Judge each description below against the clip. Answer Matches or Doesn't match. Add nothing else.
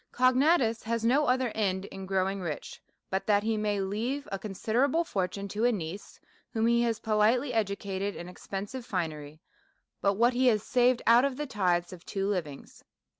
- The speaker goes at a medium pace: Matches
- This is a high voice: Matches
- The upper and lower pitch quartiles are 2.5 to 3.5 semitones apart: Doesn't match